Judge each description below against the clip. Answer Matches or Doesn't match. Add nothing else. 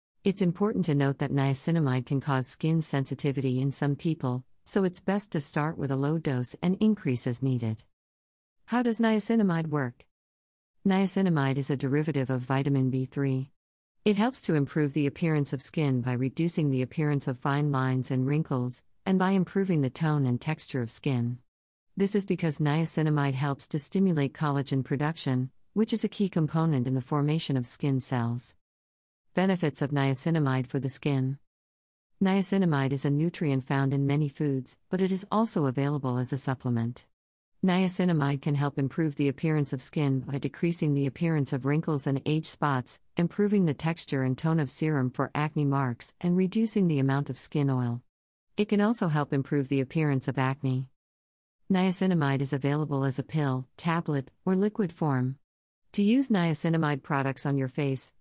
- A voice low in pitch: Doesn't match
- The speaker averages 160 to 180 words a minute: Matches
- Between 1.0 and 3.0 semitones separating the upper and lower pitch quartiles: Doesn't match